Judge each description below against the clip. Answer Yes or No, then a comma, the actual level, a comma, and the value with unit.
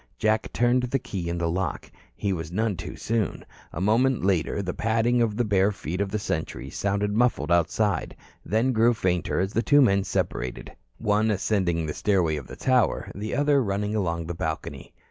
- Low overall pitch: Yes, low, 100 Hz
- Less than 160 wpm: No, average, 185 wpm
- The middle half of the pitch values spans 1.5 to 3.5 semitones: No, average, 4.3 semitones